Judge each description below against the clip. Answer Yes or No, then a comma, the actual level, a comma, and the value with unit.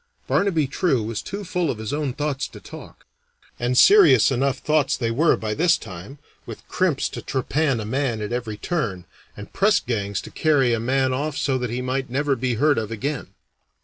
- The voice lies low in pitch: Yes, low, 130 Hz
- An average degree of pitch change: Yes, average, 4.8 semitones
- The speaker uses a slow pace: No, average, 200 wpm